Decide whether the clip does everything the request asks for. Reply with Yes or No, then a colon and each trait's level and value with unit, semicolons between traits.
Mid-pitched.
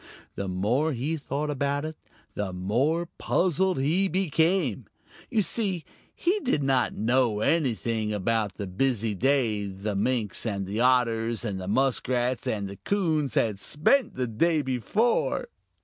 No: low, 125 Hz